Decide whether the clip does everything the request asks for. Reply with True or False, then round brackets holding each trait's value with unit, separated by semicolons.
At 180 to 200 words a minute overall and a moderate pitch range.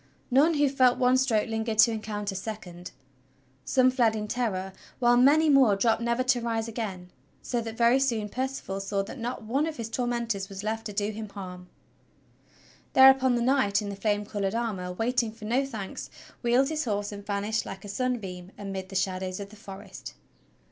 True (190 wpm; 3.7 semitones)